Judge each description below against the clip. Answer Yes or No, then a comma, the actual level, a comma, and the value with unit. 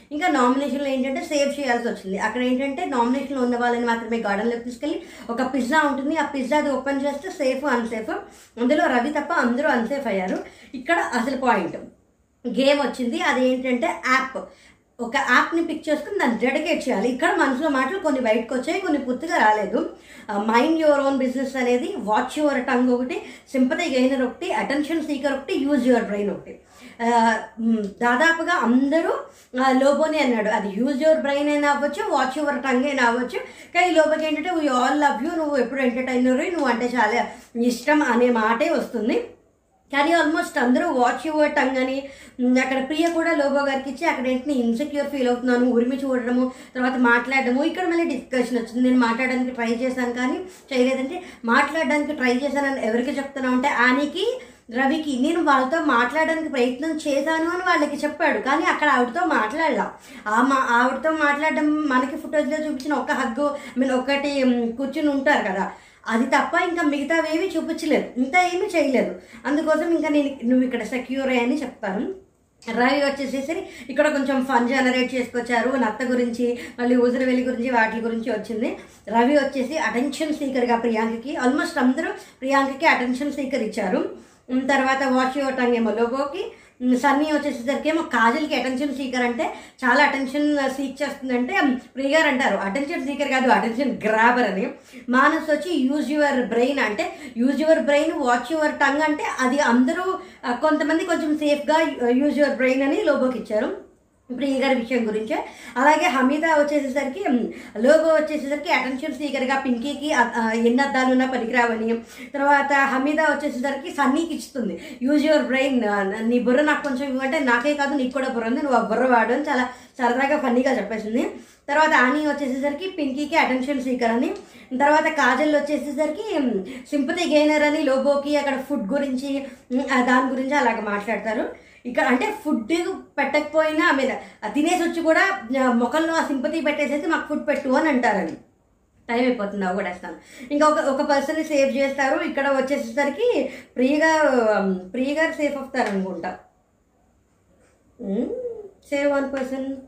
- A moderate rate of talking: No, fast, 145 wpm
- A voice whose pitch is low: No, very high, 275 Hz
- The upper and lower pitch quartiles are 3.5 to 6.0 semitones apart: No, average, 3.1 semitones